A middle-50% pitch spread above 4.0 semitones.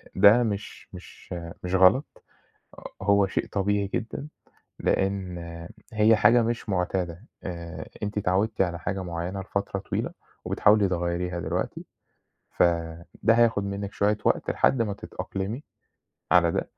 No: average, 2.8 semitones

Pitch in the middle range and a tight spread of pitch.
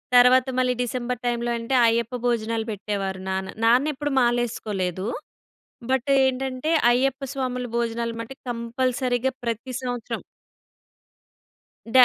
No: high, 240 Hz; narrow, 1.9 semitones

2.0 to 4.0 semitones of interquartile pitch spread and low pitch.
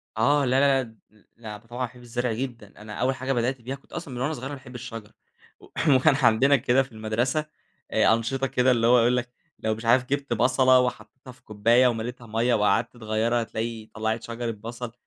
Yes: narrow, 2.4 semitones; low, 120 Hz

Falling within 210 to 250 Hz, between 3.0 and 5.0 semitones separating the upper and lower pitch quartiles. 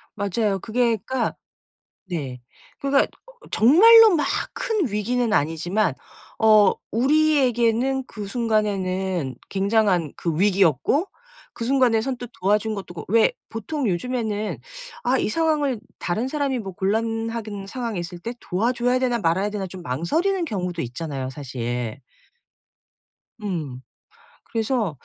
No: high, 215 Hz; wide, 5.5 semitones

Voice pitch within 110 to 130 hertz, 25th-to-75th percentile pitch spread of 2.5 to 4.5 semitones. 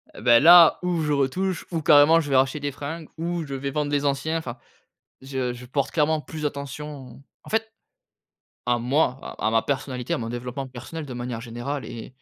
No: medium, 140 Hz; average, 3.8 semitones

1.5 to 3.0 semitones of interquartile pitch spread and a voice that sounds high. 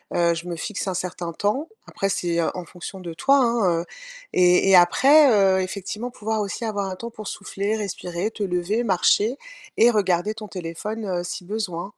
No: average, 3.6 semitones; high, 195 Hz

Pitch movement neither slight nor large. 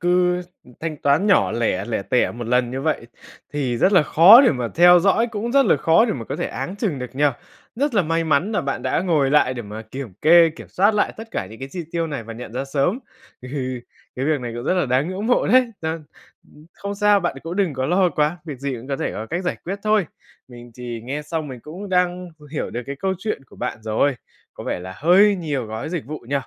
No: wide, 6.1 semitones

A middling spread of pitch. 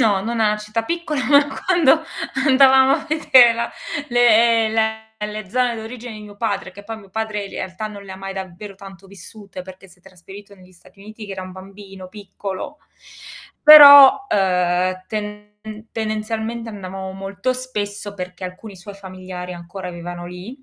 Yes: average, 3.4 semitones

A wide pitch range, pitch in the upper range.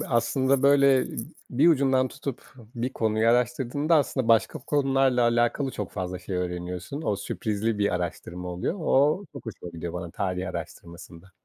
No: wide, 6.7 semitones; low, 115 Hz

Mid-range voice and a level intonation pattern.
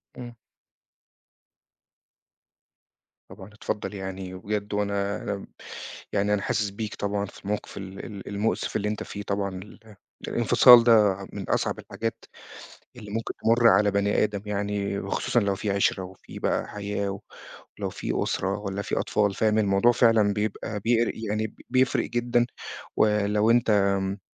No: low, 105 Hz; narrow, 1.6 semitones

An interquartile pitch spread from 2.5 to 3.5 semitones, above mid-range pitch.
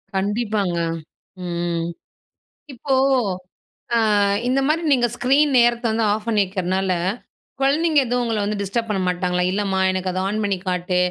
No: average, 4.5 semitones; high, 205 Hz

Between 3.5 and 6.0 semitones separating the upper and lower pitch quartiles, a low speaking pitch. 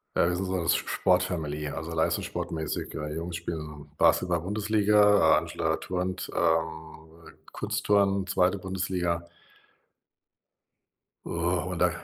No: narrow, 2.5 semitones; very low, 85 Hz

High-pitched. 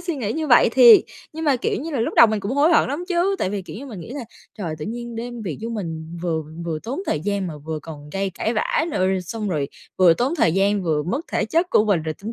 Yes: high, 210 Hz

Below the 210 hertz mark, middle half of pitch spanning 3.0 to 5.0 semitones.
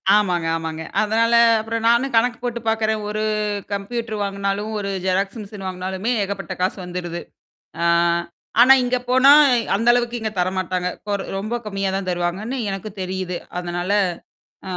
Yes: high, 200 Hz; average, 3.5 semitones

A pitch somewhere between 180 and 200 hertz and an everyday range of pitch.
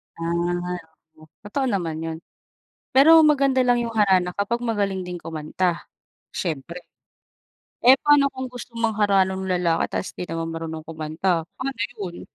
No: high, 190 Hz; wide, 6.1 semitones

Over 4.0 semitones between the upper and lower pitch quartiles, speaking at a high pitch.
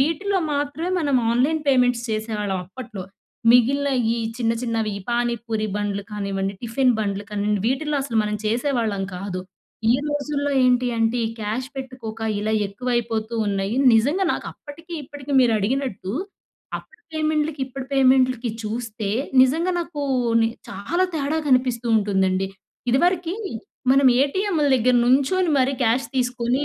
Yes: average, 4.6 semitones; very high, 250 Hz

